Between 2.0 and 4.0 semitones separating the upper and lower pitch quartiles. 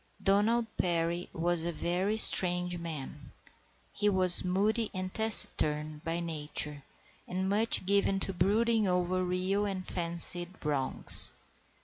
Yes: average, 2.8 semitones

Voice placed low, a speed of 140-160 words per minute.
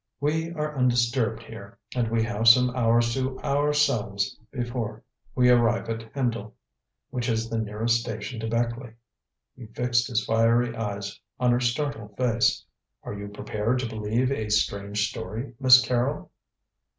Yes: low, 115 Hz; average, 150 wpm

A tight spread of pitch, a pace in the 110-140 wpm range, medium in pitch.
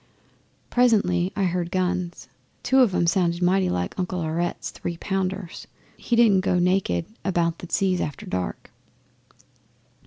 Yes: narrow, 2.0 semitones; slow, 135 wpm; medium, 180 Hz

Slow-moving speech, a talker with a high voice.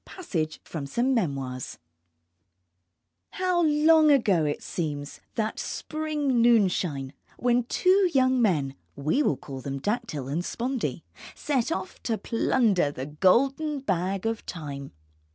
Yes: slow, 125 wpm; high, 220 Hz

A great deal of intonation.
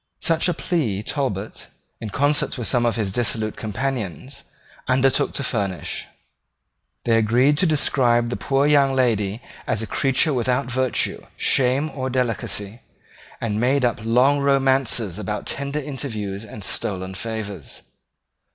No: average, 4.2 semitones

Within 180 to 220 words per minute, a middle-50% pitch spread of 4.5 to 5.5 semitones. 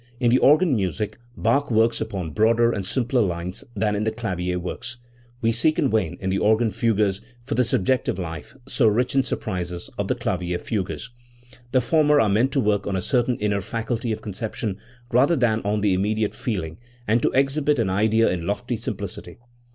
No: average, 200 wpm; average, 3.9 semitones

